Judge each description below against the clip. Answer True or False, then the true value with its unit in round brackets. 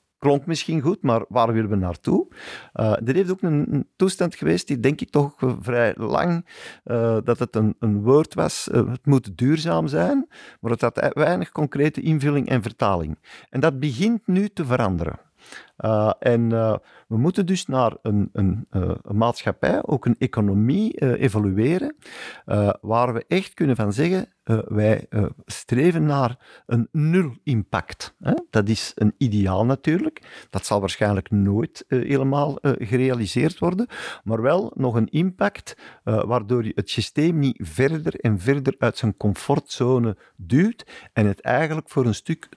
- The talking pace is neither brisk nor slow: True (165 wpm)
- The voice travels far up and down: True (6.0 semitones)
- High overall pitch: False (125 Hz)